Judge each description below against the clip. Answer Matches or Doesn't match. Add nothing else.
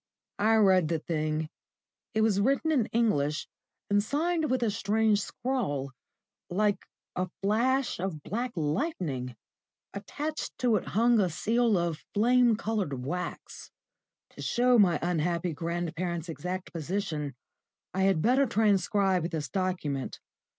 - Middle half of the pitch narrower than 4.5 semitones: Doesn't match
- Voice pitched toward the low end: Doesn't match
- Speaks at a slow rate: Matches